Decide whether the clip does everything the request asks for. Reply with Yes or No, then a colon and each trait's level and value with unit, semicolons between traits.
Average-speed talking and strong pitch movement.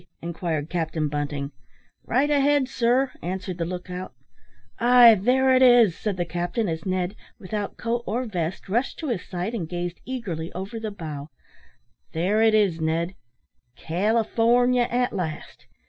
Yes: average, 150 wpm; wide, 5.8 semitones